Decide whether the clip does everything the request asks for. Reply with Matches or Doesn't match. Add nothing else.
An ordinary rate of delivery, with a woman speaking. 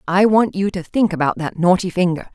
Doesn't match